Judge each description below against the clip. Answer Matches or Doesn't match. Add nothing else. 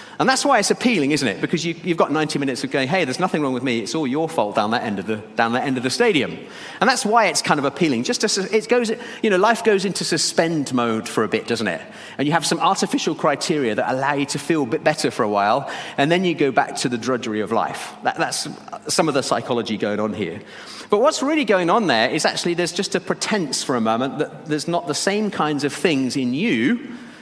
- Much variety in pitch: Matches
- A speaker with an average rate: Doesn't match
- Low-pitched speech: Doesn't match